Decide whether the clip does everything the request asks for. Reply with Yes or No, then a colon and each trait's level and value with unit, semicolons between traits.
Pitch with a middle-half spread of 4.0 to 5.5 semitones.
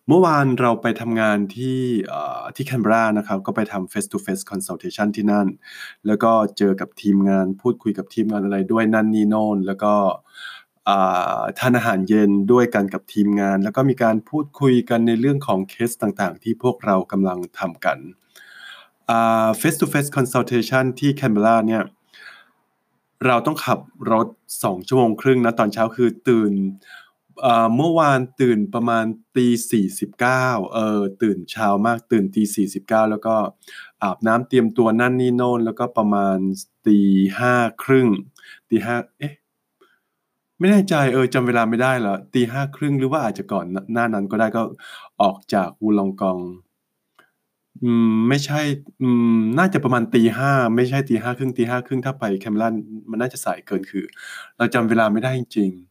No: average, 3.2 semitones